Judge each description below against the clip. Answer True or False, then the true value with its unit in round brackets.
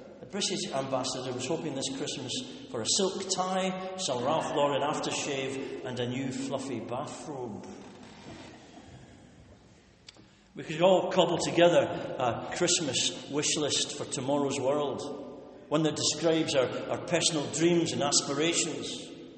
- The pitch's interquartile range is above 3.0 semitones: True (4.0 semitones)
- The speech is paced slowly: True (125 wpm)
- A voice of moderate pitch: True (150 Hz)